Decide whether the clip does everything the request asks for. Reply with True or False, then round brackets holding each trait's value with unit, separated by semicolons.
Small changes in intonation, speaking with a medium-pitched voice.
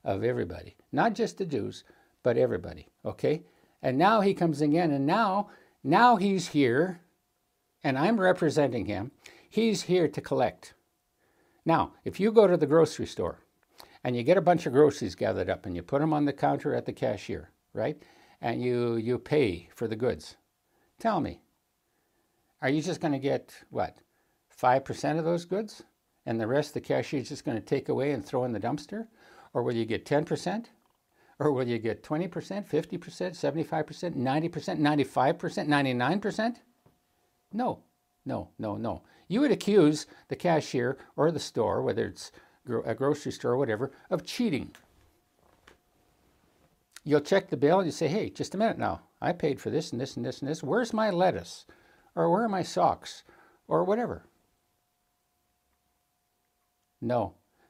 False (5.4 semitones; 155 Hz)